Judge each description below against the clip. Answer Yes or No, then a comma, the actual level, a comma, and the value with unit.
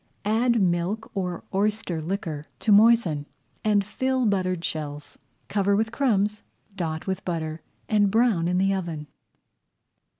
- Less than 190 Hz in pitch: No, high, 195 Hz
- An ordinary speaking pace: No, slow, 130 wpm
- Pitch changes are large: No, average, 4.0 semitones